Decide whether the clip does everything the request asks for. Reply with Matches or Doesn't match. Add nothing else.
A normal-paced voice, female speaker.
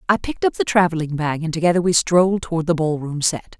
Doesn't match